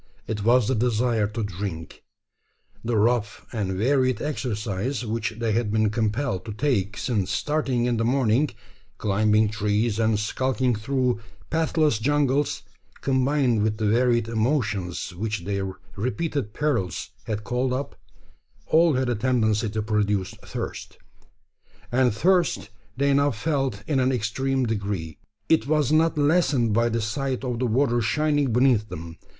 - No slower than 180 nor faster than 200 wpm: No, average, 145 wpm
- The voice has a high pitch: No, low, 115 Hz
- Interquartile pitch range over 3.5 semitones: Yes, average, 4.0 semitones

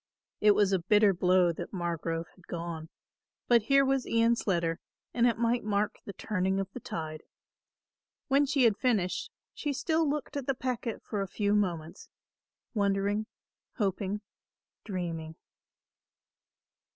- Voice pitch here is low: No, high, 205 Hz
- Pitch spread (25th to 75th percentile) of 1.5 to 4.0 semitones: No, average, 5.0 semitones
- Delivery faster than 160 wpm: No, average, 140 wpm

